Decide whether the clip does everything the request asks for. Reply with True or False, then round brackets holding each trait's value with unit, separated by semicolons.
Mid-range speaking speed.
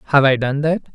False (255 wpm)